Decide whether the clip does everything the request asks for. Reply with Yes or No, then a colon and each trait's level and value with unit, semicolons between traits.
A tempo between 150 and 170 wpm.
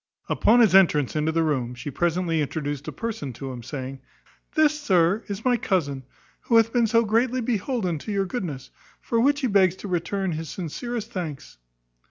No: average, 190 wpm